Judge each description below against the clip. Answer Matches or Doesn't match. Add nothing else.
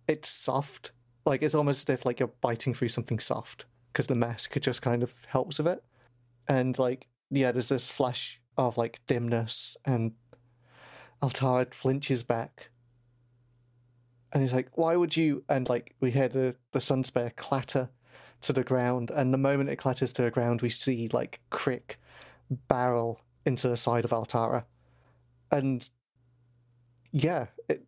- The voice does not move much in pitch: Matches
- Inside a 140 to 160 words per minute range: Matches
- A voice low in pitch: Matches